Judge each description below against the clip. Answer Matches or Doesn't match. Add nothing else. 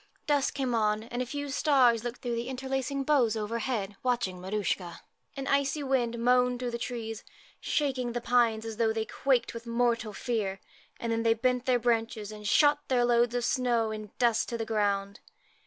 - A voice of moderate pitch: Doesn't match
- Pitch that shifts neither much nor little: Doesn't match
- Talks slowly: Doesn't match